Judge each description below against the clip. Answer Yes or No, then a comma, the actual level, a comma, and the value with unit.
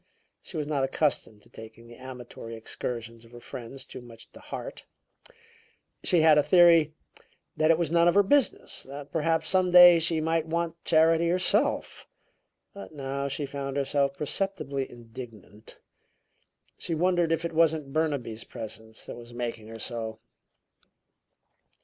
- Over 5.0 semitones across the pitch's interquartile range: Yes, wide, 5.6 semitones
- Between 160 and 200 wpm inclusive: No, average, 150 wpm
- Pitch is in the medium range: Yes, medium, 145 Hz